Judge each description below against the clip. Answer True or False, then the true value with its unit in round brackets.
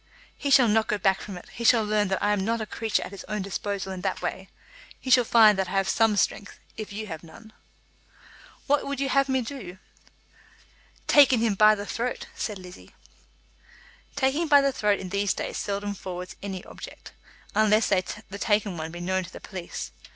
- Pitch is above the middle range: True (210 Hz)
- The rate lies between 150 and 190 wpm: False (205 wpm)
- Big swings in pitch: False (3.2 semitones)